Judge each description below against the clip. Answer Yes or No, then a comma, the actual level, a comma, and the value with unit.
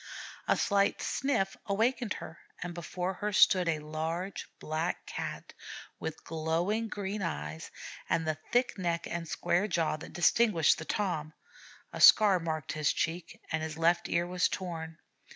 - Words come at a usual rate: Yes, average, 150 wpm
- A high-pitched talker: No, medium, 170 Hz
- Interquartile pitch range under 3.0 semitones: No, average, 3.7 semitones